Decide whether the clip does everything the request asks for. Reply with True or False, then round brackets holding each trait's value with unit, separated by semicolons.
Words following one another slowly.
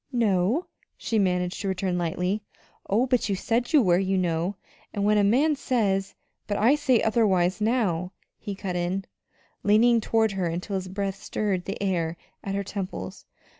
False (175 wpm)